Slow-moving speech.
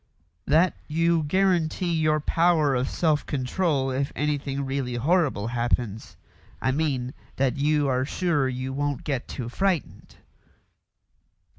Yes: slow, 125 wpm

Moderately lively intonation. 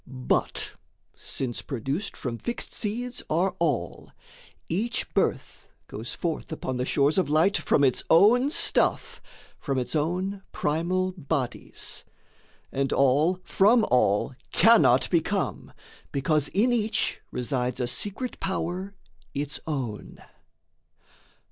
No: wide, 6.5 semitones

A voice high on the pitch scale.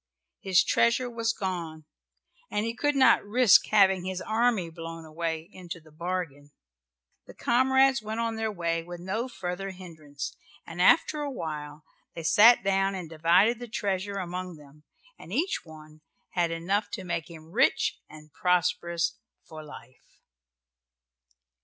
No: medium, 180 Hz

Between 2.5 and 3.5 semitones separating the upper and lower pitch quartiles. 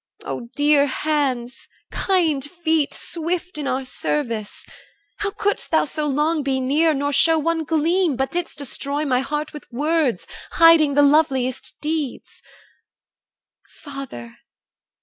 Yes: average, 3.1 semitones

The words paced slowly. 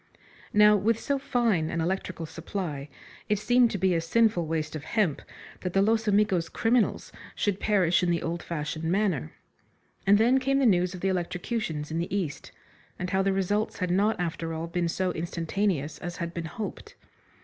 No: average, 185 wpm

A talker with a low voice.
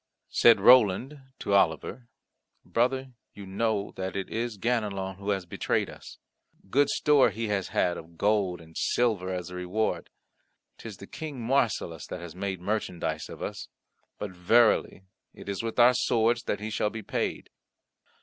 Yes: low, 105 Hz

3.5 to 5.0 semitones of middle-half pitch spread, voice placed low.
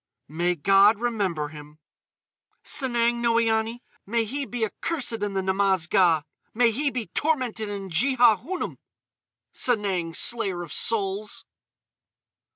No: average, 3.9 semitones; high, 215 Hz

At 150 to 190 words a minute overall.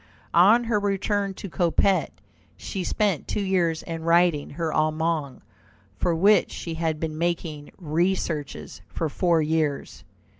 No: slow, 135 wpm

